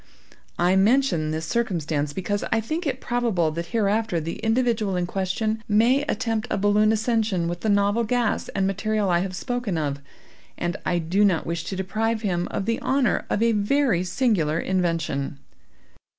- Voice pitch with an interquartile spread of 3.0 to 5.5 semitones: Yes, average, 4.5 semitones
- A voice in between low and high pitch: No, high, 200 Hz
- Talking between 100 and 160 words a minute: No, average, 170 wpm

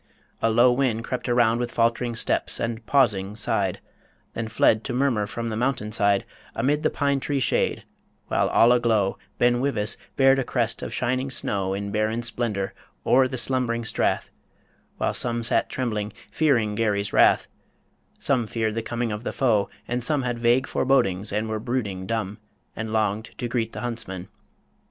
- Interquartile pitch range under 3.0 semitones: Yes, narrow, 2.6 semitones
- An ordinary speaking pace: Yes, average, 170 wpm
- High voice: No, low, 115 Hz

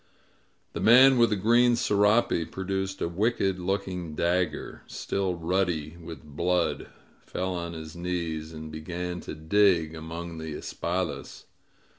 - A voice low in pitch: Yes, very low, 90 Hz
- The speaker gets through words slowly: Yes, slow, 130 wpm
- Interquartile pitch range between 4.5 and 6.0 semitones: No, average, 3.0 semitones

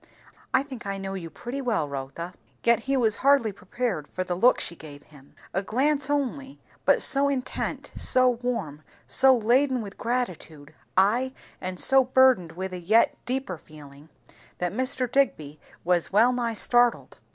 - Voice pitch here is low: No, high, 230 Hz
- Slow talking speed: No, average, 165 wpm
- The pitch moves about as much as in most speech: No, wide, 6.6 semitones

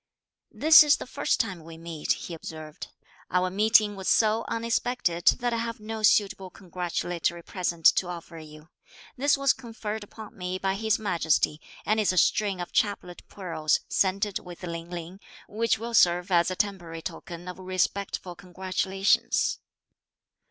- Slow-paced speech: No, average, 155 wpm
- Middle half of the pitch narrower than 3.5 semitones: No, average, 3.8 semitones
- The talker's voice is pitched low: No, medium, 185 Hz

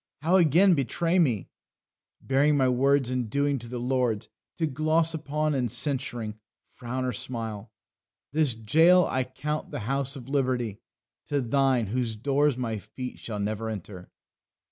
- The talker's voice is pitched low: Yes, low, 130 Hz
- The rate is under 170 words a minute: Yes, average, 150 wpm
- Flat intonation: No, average, 4.0 semitones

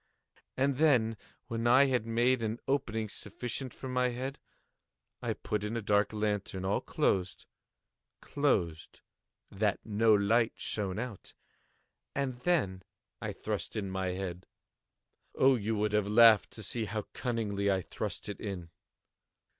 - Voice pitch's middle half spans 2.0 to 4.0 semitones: Yes, average, 3.6 semitones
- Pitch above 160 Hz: No, low, 110 Hz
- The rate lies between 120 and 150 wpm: Yes, average, 140 wpm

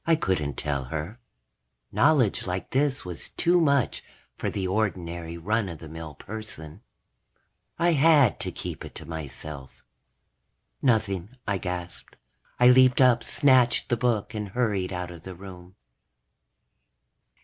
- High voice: No, low, 100 Hz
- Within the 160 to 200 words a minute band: No, average, 140 wpm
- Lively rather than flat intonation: Yes, wide, 6.6 semitones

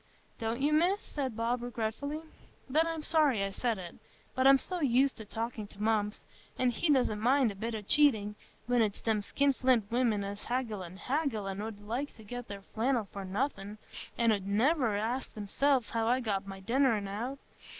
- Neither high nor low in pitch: No, high, 230 Hz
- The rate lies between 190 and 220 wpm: Yes, average, 195 wpm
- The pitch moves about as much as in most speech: Yes, average, 4.3 semitones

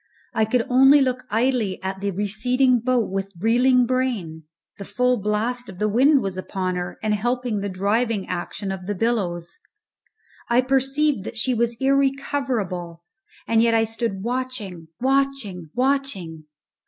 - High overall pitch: Yes, high, 225 Hz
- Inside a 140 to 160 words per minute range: Yes, average, 150 wpm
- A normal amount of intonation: Yes, average, 4.7 semitones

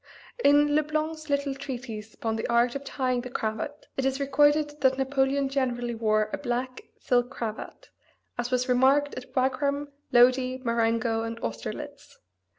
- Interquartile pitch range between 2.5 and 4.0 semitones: Yes, average, 2.9 semitones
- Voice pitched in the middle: No, very high, 255 Hz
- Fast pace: No, average, 155 wpm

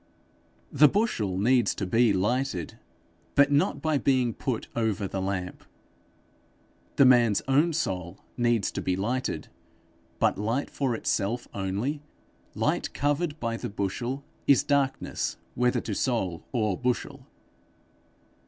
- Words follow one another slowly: Yes, slow, 125 wpm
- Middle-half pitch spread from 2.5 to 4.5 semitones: No, average, 5.2 semitones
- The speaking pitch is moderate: No, low, 120 Hz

